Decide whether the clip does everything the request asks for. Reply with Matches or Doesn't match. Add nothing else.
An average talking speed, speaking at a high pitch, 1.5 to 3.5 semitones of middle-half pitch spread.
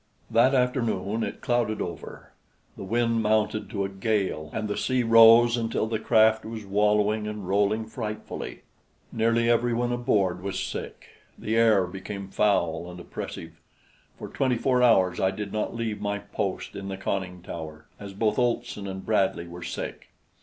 Doesn't match